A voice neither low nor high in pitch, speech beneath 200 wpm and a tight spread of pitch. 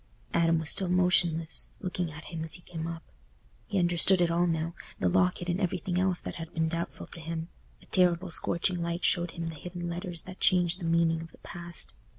No: medium, 170 Hz; fast, 205 wpm; narrow, 1.4 semitones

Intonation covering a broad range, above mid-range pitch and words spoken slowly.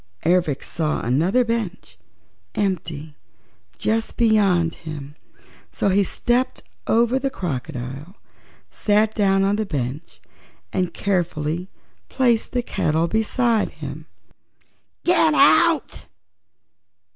Yes: wide, 6.1 semitones; high, 195 Hz; slow, 100 wpm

